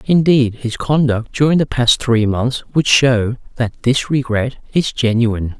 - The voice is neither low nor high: No, low, 125 Hz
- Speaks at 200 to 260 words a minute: No, average, 160 wpm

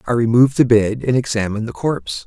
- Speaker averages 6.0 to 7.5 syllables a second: Yes, 6.6 syllables/s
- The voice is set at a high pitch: No, low, 115 Hz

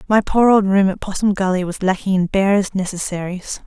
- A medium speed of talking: Yes, average, 195 wpm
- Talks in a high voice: Yes, high, 195 Hz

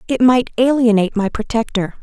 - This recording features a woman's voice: Yes, female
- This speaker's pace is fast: No, average, 150 wpm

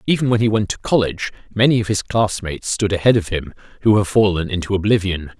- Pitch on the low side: Yes, low, 100 Hz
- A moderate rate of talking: No, fast, 210 wpm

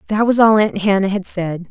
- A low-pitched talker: No, high, 200 Hz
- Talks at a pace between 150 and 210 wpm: No, fast, 245 wpm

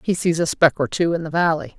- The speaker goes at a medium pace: No, fast, 300 wpm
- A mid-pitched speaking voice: Yes, medium, 165 Hz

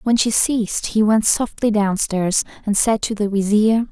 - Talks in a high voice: Yes, high, 215 Hz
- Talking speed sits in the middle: Yes, average, 185 wpm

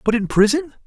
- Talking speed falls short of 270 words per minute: Yes, fast, 205 wpm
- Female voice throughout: No, male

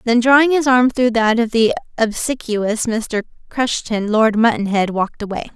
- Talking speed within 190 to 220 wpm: No, average, 160 wpm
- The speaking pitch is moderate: No, high, 230 Hz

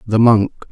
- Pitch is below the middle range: Yes, low, 110 Hz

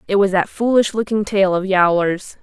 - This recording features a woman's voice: Yes, female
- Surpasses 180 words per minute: Yes, average, 200 wpm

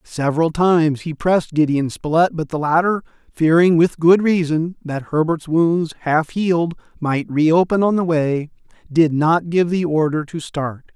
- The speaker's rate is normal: Yes, average, 165 wpm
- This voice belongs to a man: Yes, male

